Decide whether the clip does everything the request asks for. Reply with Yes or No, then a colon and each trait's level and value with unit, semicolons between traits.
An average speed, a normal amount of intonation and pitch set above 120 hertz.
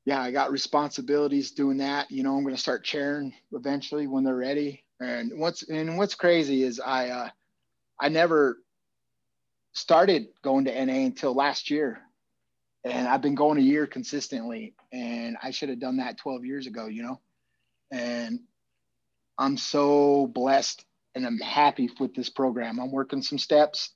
No: average, 165 wpm; narrow, 2.2 semitones; low, 135 Hz